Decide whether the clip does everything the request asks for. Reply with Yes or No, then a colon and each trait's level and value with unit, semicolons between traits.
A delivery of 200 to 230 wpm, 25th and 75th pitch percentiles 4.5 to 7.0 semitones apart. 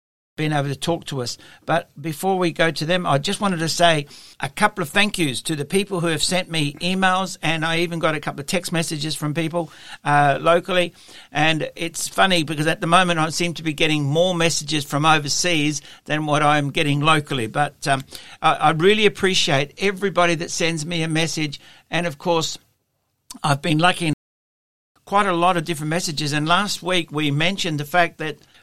No: fast, 205 wpm; average, 2.8 semitones